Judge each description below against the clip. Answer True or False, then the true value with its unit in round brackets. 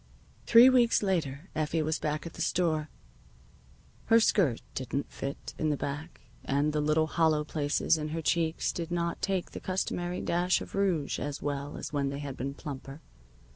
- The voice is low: False (155 Hz)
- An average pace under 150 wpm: False (175 wpm)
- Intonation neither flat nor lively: True (3.2 semitones)